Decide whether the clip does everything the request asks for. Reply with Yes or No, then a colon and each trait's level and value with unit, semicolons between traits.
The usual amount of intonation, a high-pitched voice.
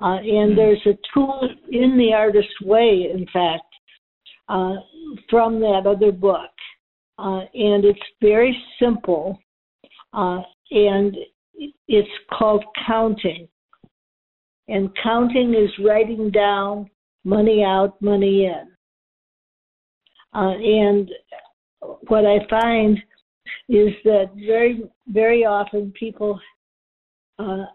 No: narrow, 2.1 semitones; high, 210 Hz